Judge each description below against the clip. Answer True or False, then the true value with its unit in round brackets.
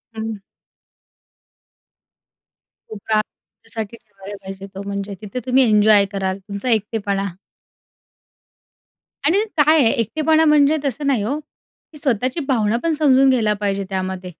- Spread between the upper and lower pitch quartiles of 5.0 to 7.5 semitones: True (5.4 semitones)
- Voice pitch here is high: True (220 Hz)